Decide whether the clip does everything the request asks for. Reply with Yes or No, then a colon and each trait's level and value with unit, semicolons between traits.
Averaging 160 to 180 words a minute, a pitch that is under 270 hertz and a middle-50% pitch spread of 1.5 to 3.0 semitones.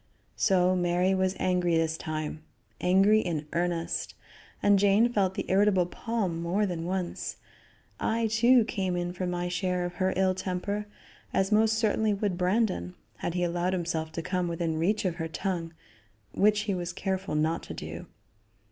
Yes: average, 165 wpm; medium, 185 Hz; average, 2.7 semitones